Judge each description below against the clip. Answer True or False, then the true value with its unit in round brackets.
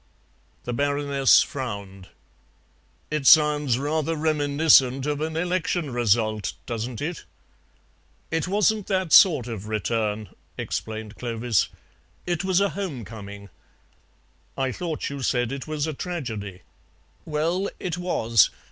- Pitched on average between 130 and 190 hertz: True (140 Hz)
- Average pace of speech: False (120 wpm)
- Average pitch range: False (6.0 semitones)